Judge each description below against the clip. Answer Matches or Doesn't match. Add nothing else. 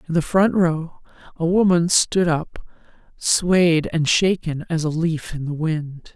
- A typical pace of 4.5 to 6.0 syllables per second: Doesn't match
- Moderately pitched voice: Matches